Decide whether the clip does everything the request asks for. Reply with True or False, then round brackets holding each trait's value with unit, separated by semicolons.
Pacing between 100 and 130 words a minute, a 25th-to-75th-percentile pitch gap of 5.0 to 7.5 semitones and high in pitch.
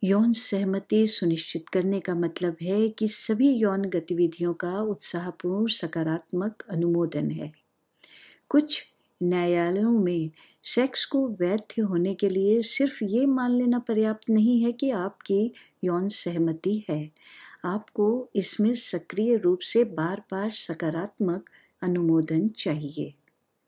False (120 wpm; 4.2 semitones; 195 Hz)